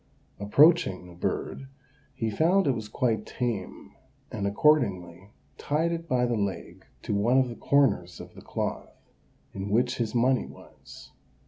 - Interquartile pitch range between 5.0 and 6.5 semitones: Yes, wide, 5.5 semitones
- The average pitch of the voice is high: No, low, 120 Hz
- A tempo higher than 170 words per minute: No, average, 150 wpm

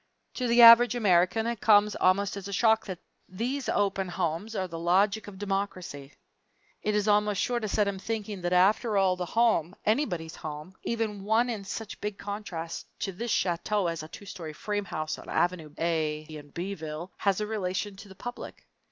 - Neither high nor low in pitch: No, high, 195 Hz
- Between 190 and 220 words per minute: Yes, average, 195 wpm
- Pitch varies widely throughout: No, average, 3.4 semitones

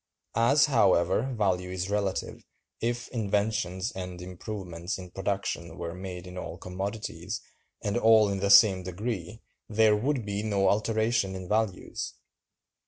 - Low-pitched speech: Yes, low, 100 Hz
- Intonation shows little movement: No, average, 3.2 semitones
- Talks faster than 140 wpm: No, slow, 135 wpm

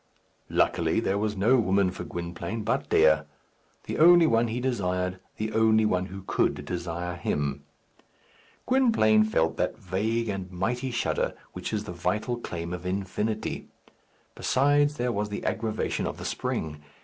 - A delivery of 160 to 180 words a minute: No, average, 150 wpm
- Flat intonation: No, average, 4.2 semitones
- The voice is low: Yes, low, 105 Hz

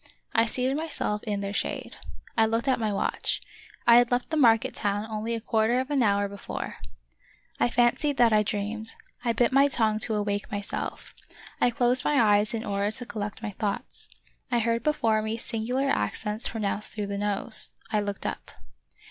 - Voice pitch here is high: Yes, high, 220 Hz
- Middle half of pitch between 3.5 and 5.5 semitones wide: No, narrow, 2.6 semitones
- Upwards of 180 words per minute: Yes, average, 190 wpm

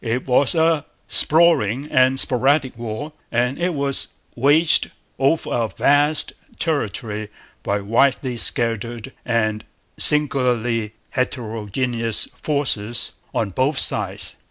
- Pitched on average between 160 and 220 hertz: No, low, 125 Hz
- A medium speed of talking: No, slow, 105 wpm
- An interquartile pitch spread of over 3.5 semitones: Yes, average, 4.0 semitones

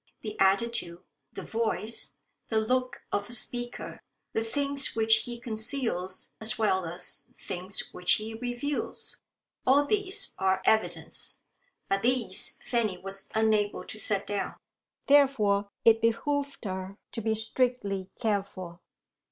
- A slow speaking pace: Yes, slow, 130 wpm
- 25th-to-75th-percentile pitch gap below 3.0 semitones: No, average, 3.6 semitones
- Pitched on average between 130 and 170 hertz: No, high, 220 Hz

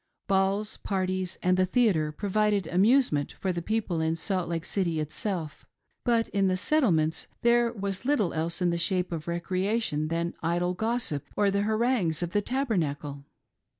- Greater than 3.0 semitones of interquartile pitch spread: Yes, average, 4.1 semitones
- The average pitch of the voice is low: No, medium, 185 Hz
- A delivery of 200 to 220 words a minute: No, average, 160 wpm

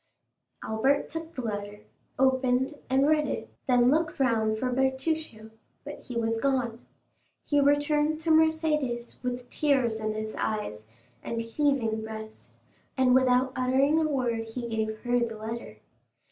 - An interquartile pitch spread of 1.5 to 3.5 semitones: No, average, 4.0 semitones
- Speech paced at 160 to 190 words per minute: No, average, 145 wpm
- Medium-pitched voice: No, very high, 250 Hz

